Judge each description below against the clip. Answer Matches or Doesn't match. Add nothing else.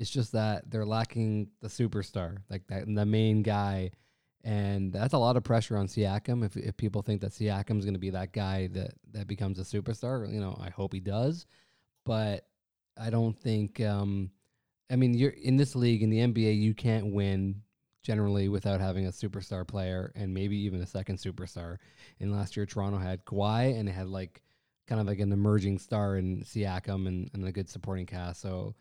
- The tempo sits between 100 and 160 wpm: Doesn't match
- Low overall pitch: Matches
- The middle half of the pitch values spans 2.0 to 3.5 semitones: Matches